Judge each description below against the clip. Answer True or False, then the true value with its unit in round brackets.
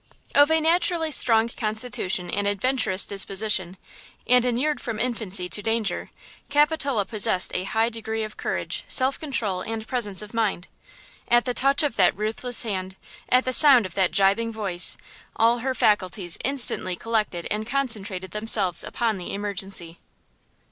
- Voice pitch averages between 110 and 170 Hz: False (220 Hz)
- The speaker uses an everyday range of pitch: True (4.3 semitones)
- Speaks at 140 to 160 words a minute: True (150 wpm)